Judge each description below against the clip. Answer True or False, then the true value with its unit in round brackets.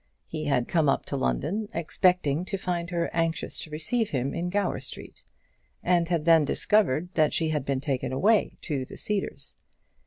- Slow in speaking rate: False (180 wpm)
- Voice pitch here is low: False (165 Hz)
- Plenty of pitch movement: False (4.2 semitones)